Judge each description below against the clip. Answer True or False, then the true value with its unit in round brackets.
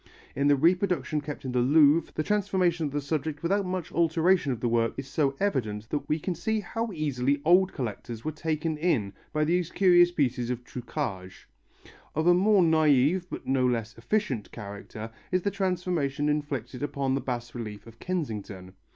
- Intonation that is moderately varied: False (5.9 semitones)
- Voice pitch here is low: False (150 Hz)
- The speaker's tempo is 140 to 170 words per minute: False (180 wpm)